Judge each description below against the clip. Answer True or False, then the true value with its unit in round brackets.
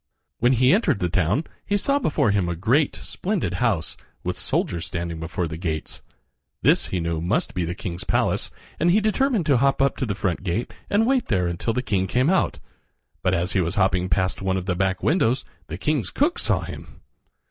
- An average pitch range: False (7.9 semitones)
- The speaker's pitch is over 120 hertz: False (95 Hz)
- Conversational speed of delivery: False (210 wpm)